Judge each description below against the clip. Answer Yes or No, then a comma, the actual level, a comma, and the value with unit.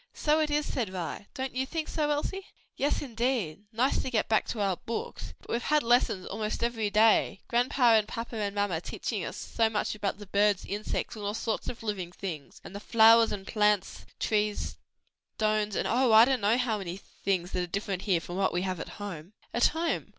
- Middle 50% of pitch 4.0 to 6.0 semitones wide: No, average, 3.4 semitones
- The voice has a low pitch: No, high, 215 Hz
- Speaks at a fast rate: Yes, fast, 215 wpm